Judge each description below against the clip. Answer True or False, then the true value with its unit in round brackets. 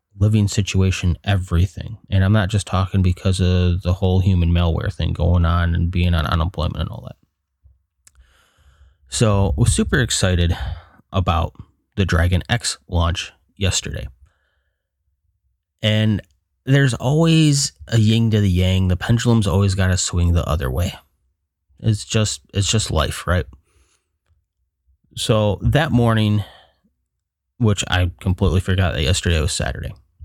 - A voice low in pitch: True (90 Hz)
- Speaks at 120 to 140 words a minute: True (135 wpm)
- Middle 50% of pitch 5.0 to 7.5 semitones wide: False (4.1 semitones)